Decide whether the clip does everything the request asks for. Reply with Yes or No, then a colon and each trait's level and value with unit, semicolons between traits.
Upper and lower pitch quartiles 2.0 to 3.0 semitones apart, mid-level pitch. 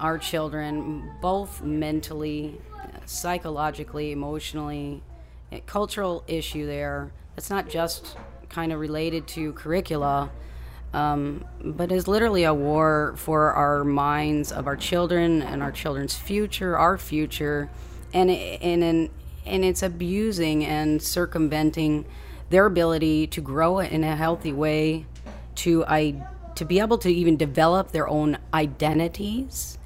Yes: narrow, 2.5 semitones; medium, 155 Hz